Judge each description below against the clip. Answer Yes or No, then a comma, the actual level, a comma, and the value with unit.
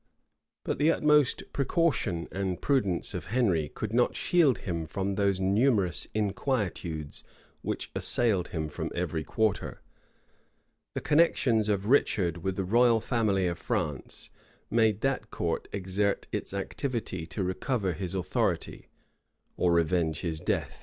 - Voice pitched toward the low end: Yes, low, 100 Hz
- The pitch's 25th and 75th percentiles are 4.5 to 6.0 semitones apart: Yes, average, 5.1 semitones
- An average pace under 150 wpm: Yes, slow, 135 wpm